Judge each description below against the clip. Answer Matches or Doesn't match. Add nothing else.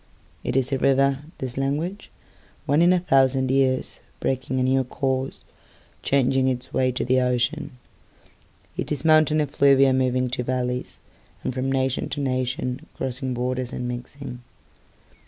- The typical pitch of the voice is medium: Doesn't match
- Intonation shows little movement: Matches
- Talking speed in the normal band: Doesn't match